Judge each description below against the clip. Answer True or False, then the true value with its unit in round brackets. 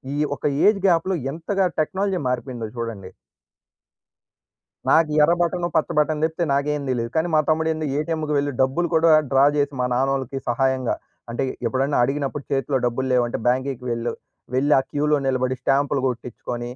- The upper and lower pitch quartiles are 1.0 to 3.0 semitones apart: False (3.7 semitones)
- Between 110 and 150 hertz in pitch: True (140 Hz)